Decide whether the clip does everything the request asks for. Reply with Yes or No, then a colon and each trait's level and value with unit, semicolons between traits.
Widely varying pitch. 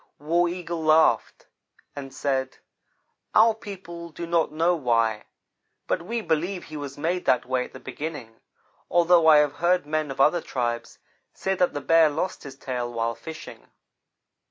No: average, 4.4 semitones